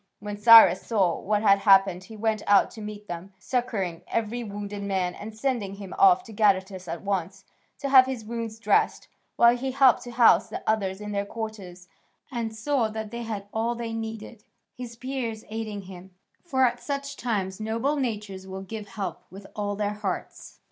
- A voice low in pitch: No, high, 215 Hz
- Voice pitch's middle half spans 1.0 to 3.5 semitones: Yes, average, 2.9 semitones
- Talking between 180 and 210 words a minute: Yes, average, 185 wpm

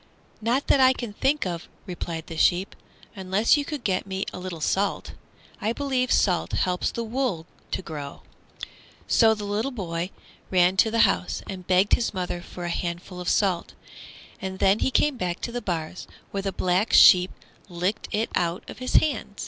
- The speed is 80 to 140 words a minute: No, average, 180 wpm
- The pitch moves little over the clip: No, average, 4.3 semitones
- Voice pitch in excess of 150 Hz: Yes, high, 190 Hz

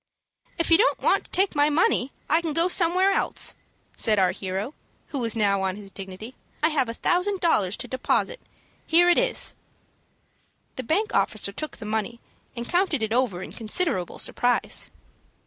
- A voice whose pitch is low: No, very high, 255 Hz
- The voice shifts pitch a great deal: Yes, wide, 8.2 semitones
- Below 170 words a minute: No, average, 175 wpm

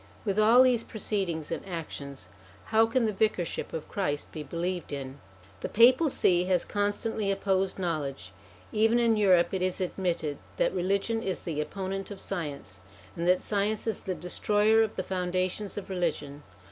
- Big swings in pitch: No, average, 3.9 semitones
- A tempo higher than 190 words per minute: No, average, 165 wpm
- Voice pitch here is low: No, high, 190 Hz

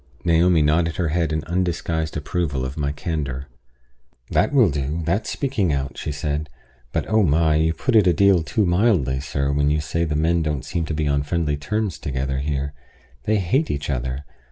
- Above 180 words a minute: Yes, average, 195 wpm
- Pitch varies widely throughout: No, average, 3.3 semitones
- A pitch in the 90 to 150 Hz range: No, very low, 80 Hz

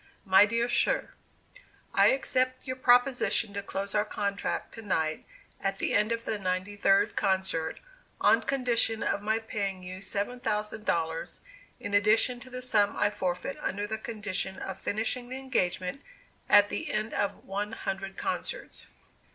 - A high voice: Yes, high, 210 Hz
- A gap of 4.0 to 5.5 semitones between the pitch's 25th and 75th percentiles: No, average, 3.3 semitones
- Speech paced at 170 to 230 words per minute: No, average, 160 wpm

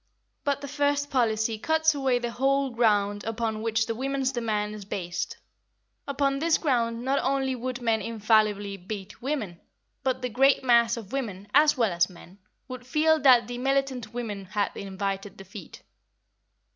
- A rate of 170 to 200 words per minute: No, average, 160 wpm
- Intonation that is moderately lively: Yes, average, 4.5 semitones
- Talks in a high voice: Yes, high, 235 Hz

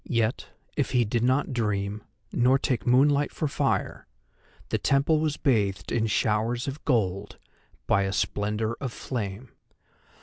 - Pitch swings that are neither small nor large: Yes, average, 4.3 semitones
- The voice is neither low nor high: No, low, 120 Hz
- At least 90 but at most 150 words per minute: Yes, average, 140 wpm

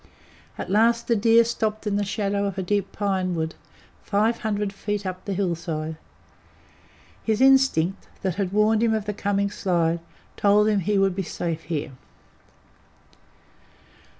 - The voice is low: No, high, 200 Hz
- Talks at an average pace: Yes, average, 150 wpm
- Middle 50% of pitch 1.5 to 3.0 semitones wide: Yes, narrow, 2.6 semitones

